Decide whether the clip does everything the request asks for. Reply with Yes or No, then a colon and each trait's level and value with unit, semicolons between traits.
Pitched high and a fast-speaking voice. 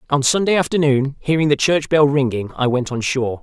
No: medium, 140 Hz; fast, 210 wpm